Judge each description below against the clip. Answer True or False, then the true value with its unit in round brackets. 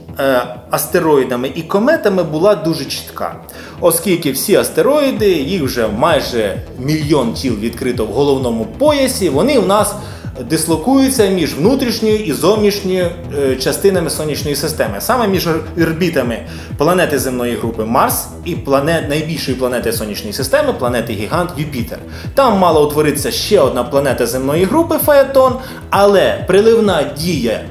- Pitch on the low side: False (160 Hz)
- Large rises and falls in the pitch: True (7.7 semitones)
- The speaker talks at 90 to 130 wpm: True (125 wpm)